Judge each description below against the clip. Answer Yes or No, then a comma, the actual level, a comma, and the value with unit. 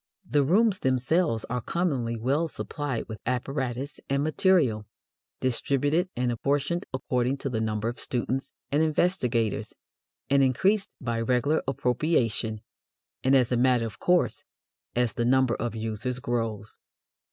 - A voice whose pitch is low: Yes, low, 130 Hz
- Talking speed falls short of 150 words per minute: Yes, slow, 135 wpm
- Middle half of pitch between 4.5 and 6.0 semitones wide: No, average, 3.7 semitones